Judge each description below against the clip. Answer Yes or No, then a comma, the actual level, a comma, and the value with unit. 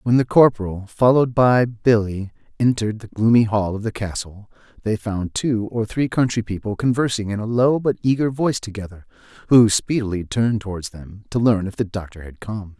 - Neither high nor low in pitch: No, low, 110 Hz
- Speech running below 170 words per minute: No, average, 190 wpm